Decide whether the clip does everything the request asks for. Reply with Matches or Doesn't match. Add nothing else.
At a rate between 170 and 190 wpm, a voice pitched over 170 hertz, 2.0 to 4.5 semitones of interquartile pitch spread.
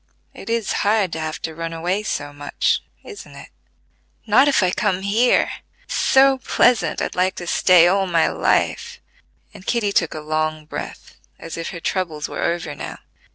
Doesn't match